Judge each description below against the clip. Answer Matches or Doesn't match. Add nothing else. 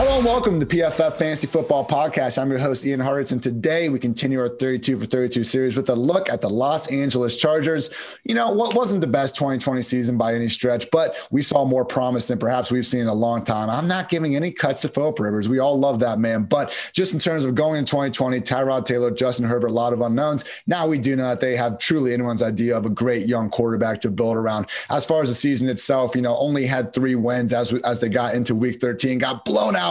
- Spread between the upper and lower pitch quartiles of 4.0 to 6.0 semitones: Doesn't match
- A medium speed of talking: Doesn't match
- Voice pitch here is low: Matches